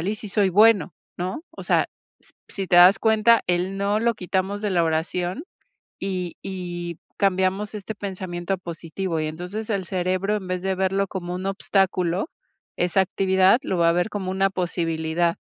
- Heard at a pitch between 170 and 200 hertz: Yes, medium, 185 Hz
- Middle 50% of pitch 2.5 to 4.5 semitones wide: No, narrow, 2.1 semitones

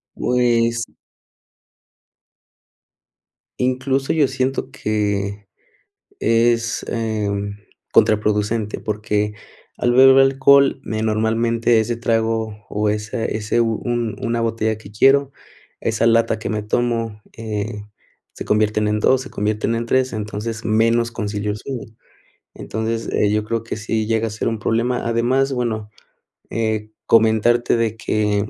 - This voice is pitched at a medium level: No, low, 115 Hz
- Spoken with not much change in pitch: Yes, narrow, 1.8 semitones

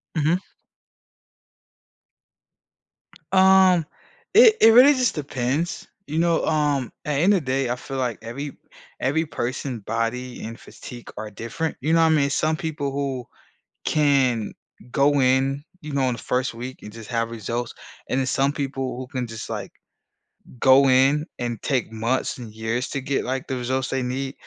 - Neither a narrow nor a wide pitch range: Yes, average, 3.4 semitones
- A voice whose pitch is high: No, low, 135 Hz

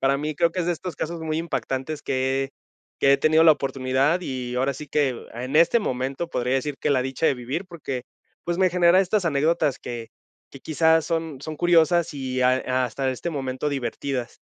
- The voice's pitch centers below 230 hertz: Yes, medium, 140 Hz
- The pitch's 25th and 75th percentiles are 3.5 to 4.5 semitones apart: Yes, average, 4.0 semitones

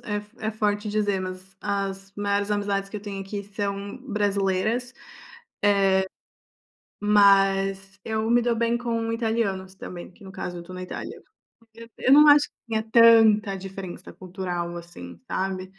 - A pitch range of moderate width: No, narrow, 2.3 semitones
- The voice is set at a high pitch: Yes, high, 200 Hz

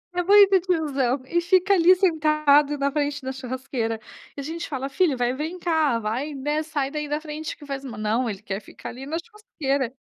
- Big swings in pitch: No, average, 3.8 semitones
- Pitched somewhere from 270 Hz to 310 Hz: Yes, very high, 290 Hz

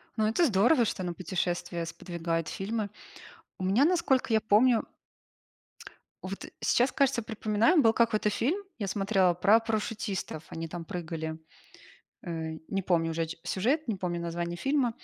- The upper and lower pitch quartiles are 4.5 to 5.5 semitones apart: Yes, average, 5.0 semitones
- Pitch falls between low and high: No, high, 200 Hz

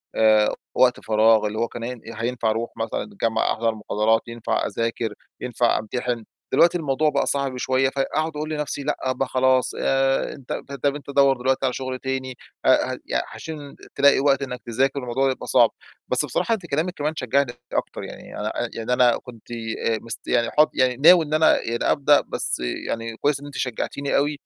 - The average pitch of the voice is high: No, low, 130 Hz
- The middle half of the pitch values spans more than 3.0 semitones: Yes, average, 3.4 semitones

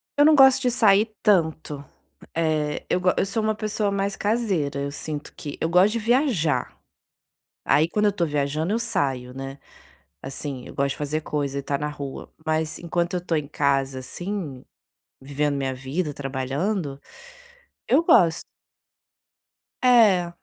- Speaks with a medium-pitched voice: Yes, medium, 160 Hz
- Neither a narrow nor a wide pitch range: No, wide, 6.3 semitones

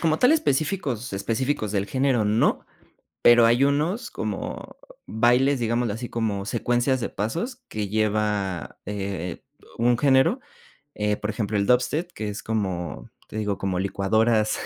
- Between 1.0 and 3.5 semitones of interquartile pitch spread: No, average, 4.3 semitones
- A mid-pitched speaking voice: No, low, 110 Hz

